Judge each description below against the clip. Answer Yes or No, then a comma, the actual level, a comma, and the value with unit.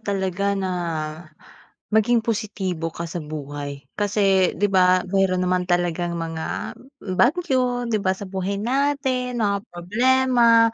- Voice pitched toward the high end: Yes, high, 200 Hz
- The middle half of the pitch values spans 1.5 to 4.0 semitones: No, average, 4.6 semitones